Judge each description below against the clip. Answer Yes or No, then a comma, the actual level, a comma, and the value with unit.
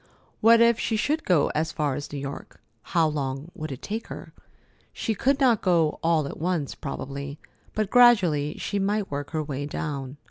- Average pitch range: No, wide, 6.6 semitones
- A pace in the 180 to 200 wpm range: Yes, average, 185 wpm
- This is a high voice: No, medium, 160 Hz